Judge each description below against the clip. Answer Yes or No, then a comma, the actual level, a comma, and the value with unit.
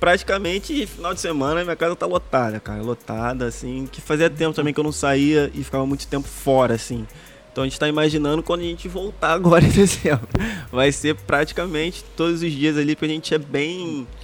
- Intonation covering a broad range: No, average, 3.8 semitones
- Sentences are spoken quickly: Yes, fast, 205 wpm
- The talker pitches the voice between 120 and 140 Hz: No, medium, 150 Hz